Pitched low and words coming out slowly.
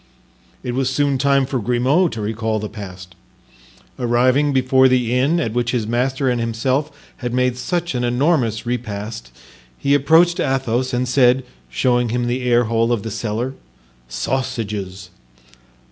No: low, 125 Hz; average, 145 wpm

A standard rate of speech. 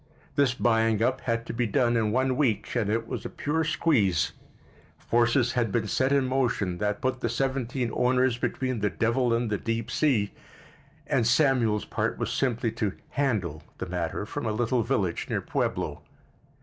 Yes: average, 175 wpm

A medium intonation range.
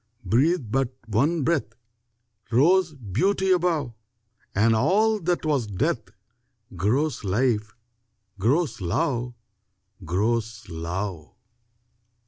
No: wide, 7.4 semitones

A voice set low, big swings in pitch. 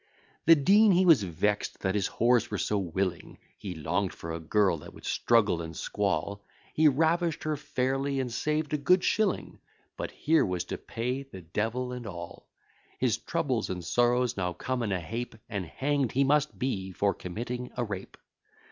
Yes: low, 120 Hz; wide, 6.5 semitones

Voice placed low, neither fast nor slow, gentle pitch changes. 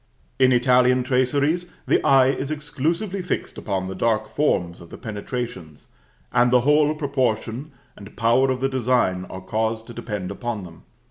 No: low, 125 Hz; average, 160 wpm; average, 4.1 semitones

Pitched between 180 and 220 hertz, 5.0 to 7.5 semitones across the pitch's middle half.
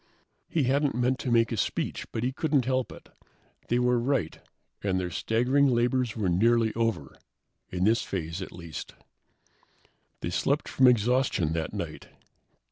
No: low, 120 Hz; average, 5.3 semitones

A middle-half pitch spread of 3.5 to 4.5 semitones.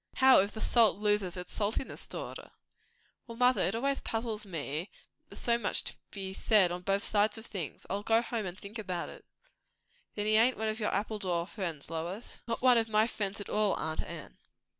No: average, 3.1 semitones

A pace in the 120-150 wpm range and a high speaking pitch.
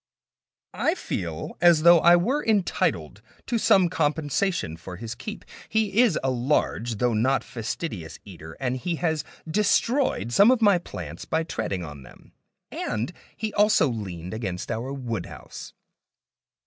No: average, 145 wpm; low, 135 Hz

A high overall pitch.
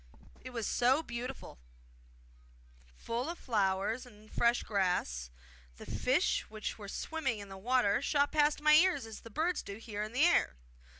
Yes: high, 240 Hz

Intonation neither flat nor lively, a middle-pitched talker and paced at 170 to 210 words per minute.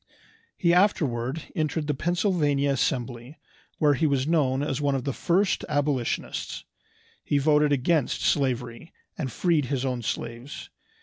No: average, 3.3 semitones; medium, 145 Hz; slow, 135 wpm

